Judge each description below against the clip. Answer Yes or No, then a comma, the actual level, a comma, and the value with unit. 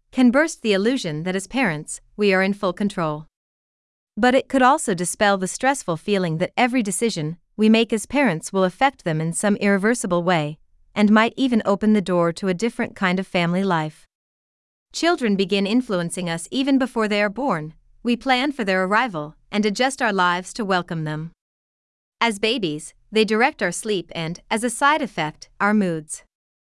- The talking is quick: No, average, 180 wpm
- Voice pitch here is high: Yes, high, 205 Hz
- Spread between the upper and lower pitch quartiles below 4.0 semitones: No, average, 4.9 semitones